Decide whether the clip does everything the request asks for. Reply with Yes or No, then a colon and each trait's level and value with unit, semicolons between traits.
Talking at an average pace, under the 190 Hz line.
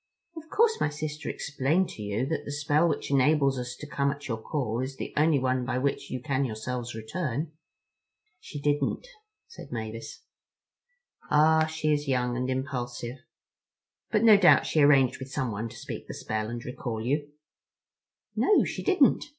Yes: average, 170 wpm; medium, 140 Hz